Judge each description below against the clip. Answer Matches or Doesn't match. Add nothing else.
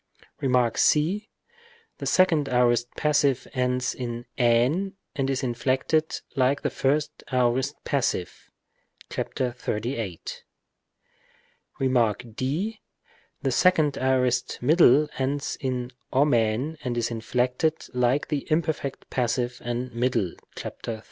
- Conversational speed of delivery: Doesn't match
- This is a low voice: Matches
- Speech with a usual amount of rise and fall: Matches